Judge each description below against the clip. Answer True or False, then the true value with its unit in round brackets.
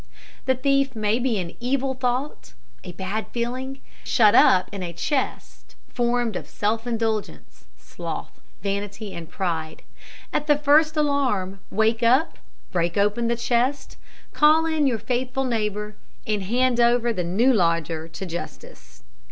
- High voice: True (230 Hz)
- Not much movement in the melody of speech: False (4.7 semitones)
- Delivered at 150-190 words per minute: False (140 wpm)